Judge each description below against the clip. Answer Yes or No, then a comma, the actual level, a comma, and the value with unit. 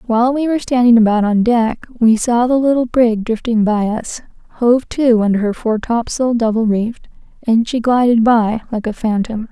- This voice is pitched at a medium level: No, high, 230 Hz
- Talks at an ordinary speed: Yes, average, 190 wpm